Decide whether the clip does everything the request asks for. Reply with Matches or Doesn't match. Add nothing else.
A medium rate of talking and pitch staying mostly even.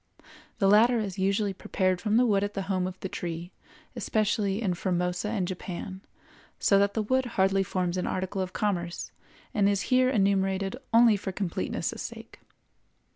Matches